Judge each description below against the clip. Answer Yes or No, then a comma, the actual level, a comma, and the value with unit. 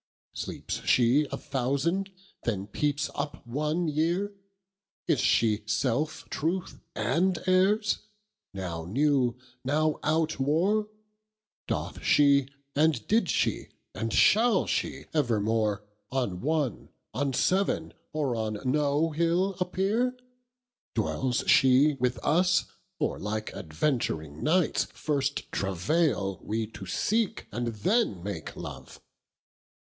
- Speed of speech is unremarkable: No, slow, 110 wpm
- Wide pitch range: Yes, wide, 6.9 semitones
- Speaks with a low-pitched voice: No, medium, 145 Hz